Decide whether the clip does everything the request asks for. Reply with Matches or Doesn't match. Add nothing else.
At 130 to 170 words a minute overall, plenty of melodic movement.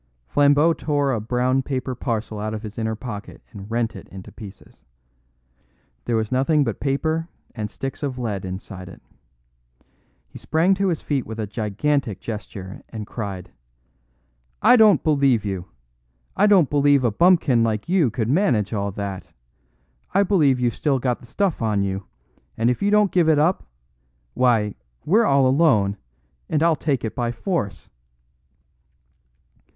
Matches